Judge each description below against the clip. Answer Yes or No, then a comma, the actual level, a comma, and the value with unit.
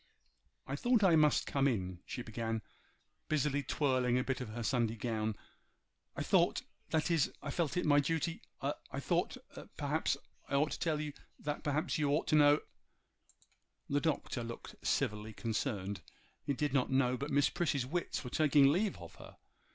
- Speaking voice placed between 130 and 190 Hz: Yes, medium, 140 Hz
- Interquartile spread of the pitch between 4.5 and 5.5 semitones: No, average, 3.9 semitones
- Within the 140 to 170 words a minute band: Yes, average, 160 wpm